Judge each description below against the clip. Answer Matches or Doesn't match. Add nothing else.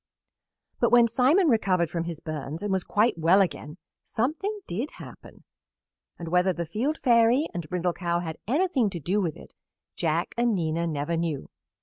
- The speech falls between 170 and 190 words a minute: Matches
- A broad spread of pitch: Matches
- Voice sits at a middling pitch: Matches